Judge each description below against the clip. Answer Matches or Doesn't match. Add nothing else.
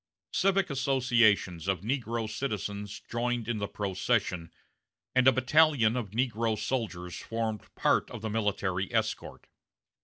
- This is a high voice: Doesn't match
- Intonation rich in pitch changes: Doesn't match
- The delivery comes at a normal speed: Doesn't match